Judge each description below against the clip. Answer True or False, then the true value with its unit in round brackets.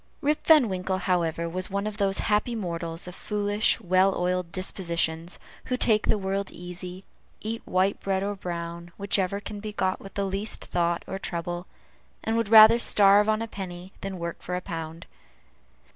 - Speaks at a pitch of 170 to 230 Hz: True (190 Hz)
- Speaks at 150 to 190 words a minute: True (175 wpm)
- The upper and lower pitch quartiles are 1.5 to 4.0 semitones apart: True (2.8 semitones)